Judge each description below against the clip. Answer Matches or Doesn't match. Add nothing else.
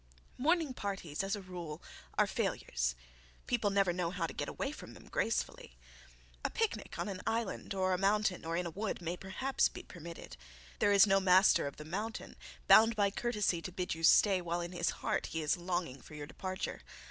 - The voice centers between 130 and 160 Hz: Doesn't match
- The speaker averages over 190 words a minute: Matches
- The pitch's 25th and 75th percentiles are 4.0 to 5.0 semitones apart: Doesn't match